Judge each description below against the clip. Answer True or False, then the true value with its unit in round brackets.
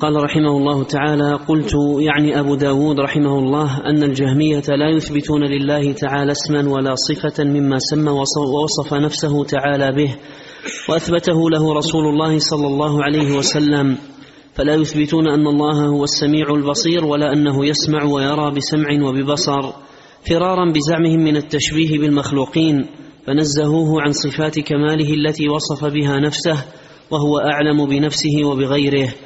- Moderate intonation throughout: False (1.1 semitones)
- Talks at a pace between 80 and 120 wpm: False (130 wpm)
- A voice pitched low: False (150 Hz)